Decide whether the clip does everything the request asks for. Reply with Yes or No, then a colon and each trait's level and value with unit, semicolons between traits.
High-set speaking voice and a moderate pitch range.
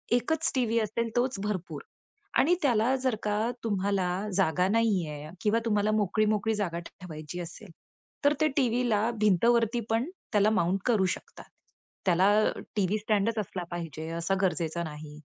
Yes: high, 205 Hz; average, 4.3 semitones